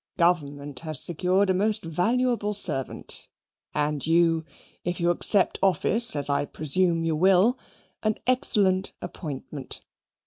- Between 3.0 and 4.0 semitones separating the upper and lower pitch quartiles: No, average, 4.8 semitones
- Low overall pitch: No, medium, 175 Hz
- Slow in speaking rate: Yes, slow, 125 wpm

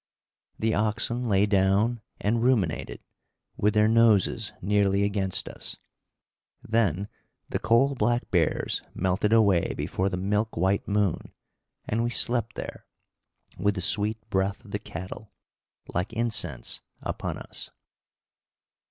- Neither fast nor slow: No, slow, 125 wpm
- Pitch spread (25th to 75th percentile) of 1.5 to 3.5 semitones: Yes, average, 2.8 semitones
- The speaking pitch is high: No, low, 105 Hz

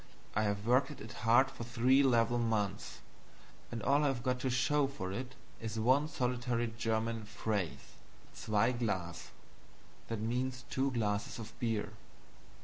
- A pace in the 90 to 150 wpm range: Yes, average, 145 wpm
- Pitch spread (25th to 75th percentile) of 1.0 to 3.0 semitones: Yes, narrow, 2.6 semitones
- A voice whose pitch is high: No, low, 115 Hz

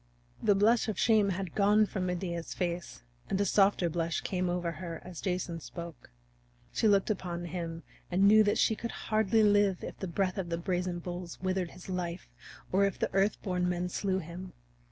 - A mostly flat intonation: Yes, narrow, 2.3 semitones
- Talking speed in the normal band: Yes, average, 195 wpm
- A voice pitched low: No, medium, 185 Hz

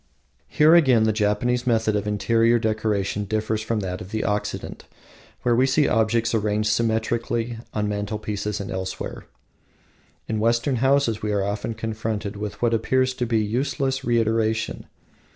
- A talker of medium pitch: No, low, 110 Hz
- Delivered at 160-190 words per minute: No, average, 150 wpm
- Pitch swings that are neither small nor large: No, narrow, 2.0 semitones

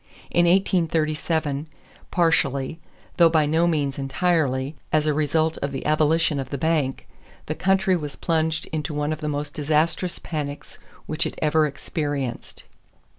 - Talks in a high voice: No, medium, 155 Hz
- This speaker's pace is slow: No, average, 145 wpm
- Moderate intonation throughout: No, narrow, 2.1 semitones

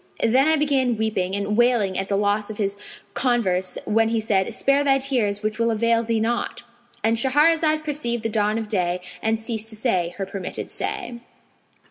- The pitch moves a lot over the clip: No, average, 3.3 semitones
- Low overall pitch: No, high, 225 Hz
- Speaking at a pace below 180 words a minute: No, average, 185 wpm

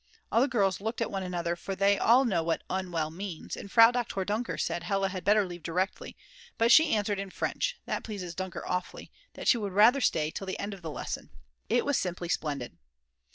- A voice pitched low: No, high, 195 Hz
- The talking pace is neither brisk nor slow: No, fast, 215 wpm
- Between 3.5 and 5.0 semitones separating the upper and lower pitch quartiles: Yes, average, 3.8 semitones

